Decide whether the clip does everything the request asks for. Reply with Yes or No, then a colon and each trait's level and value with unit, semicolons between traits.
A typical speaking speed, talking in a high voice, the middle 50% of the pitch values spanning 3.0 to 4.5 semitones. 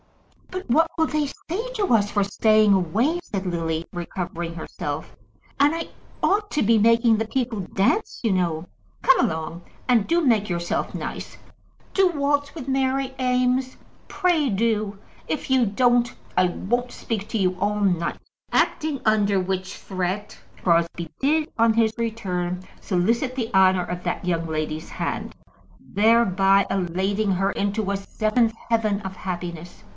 No: average, 150 wpm; high, 210 Hz; wide, 5.5 semitones